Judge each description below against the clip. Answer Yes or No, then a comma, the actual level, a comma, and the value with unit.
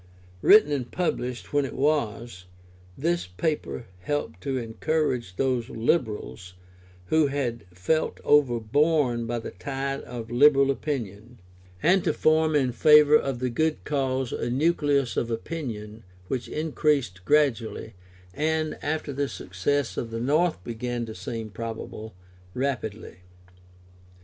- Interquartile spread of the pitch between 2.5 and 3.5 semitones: No, average, 4.7 semitones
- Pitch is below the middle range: Yes, low, 130 Hz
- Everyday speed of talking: No, slow, 130 wpm